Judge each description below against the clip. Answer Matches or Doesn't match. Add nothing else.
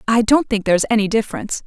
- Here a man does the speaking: Doesn't match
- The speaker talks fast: Matches